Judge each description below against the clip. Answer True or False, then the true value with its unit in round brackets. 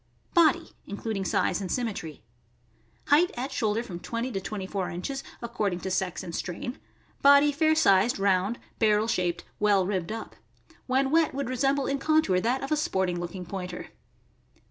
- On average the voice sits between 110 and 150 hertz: False (215 Hz)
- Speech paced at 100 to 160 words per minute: False (170 wpm)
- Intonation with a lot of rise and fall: True (6.4 semitones)